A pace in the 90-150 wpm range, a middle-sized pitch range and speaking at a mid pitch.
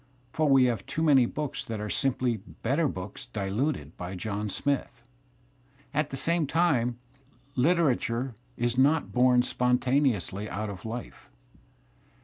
No: average, 140 wpm; average, 4.4 semitones; low, 125 Hz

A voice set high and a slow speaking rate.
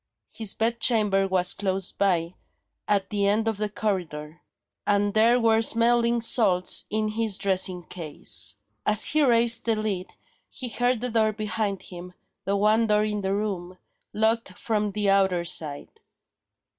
No: high, 210 Hz; average, 155 wpm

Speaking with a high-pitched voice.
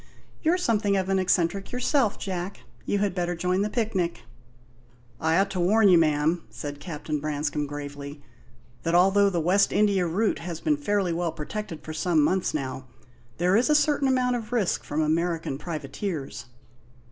No: medium, 180 Hz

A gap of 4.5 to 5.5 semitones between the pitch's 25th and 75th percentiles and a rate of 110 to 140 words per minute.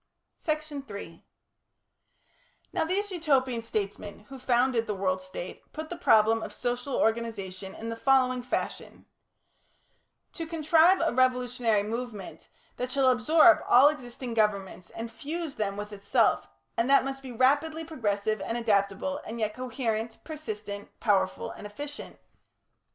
Yes: average, 4.9 semitones; slow, 135 wpm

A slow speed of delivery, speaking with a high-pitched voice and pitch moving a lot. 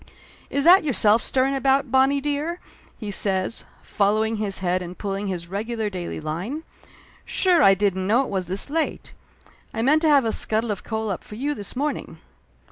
No: average, 185 wpm; high, 220 Hz; wide, 6.0 semitones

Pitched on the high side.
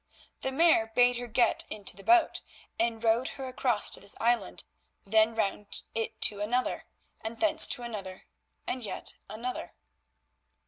Yes: high, 230 Hz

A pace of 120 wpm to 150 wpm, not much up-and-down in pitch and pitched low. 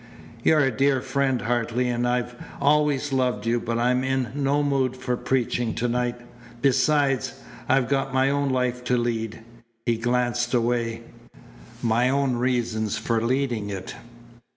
Yes: average, 145 wpm; narrow, 2.1 semitones; low, 125 Hz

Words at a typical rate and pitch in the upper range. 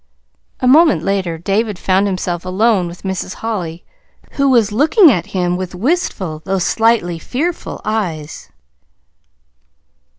No: slow, 125 wpm; high, 195 Hz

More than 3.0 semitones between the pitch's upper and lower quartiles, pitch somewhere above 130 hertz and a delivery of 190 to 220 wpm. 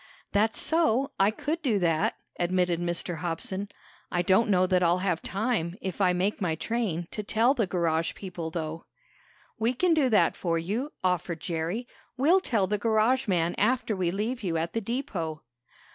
No: average, 4.9 semitones; high, 190 Hz; average, 175 wpm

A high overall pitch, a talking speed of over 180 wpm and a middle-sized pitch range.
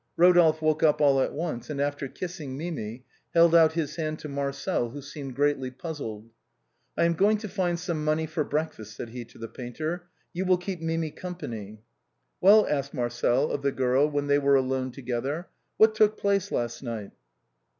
No: medium, 150 Hz; average, 200 wpm; average, 4.5 semitones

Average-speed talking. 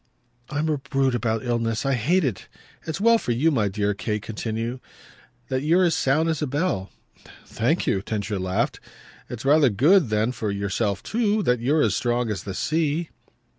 Yes: average, 180 wpm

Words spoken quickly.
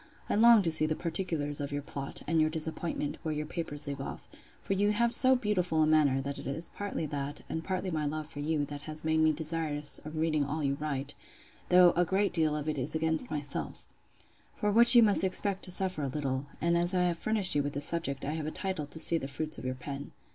Yes: fast, 245 wpm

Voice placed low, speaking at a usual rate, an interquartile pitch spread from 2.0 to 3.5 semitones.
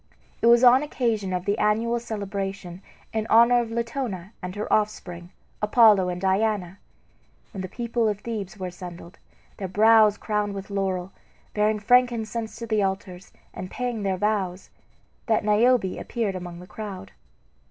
No: high, 210 Hz; average, 155 wpm; average, 3.2 semitones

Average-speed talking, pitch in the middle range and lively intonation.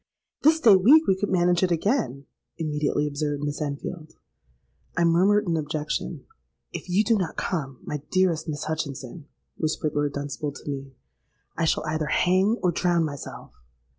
No: average, 150 wpm; medium, 160 Hz; average, 4.1 semitones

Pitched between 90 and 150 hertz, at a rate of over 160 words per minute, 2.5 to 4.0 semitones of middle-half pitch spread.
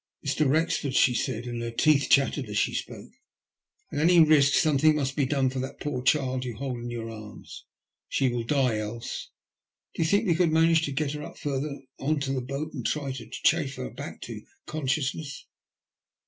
Yes: medium, 140 Hz; fast, 205 wpm; average, 3.3 semitones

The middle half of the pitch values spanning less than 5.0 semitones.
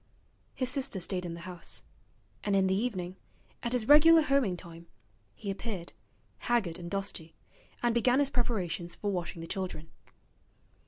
No: wide, 5.6 semitones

